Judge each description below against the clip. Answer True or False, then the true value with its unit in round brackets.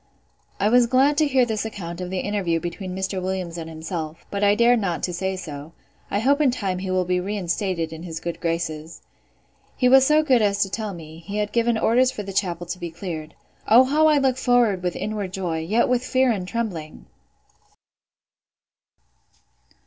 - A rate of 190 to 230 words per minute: True (195 wpm)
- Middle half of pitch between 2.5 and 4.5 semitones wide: False (5.4 semitones)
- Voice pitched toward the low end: False (195 Hz)